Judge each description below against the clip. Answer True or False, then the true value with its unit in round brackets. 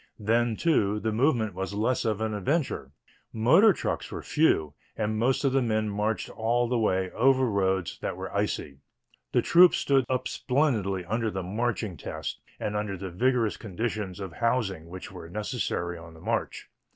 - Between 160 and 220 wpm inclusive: True (175 wpm)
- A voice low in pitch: True (110 Hz)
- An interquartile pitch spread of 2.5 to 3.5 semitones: False (4.2 semitones)